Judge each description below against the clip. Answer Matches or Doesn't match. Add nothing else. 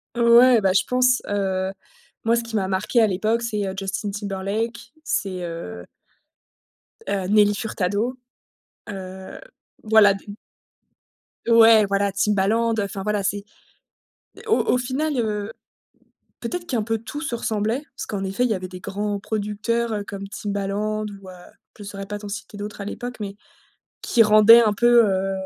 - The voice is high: Matches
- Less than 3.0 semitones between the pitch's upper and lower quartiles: Matches